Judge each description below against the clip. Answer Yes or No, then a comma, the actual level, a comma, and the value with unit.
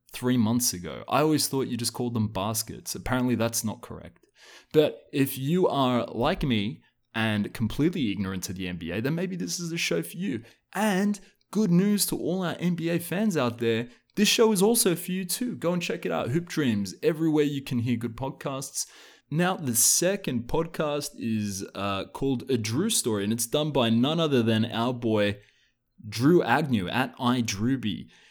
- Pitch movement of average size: No, wide, 6.8 semitones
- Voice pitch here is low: Yes, low, 130 Hz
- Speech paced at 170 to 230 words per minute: Yes, average, 185 wpm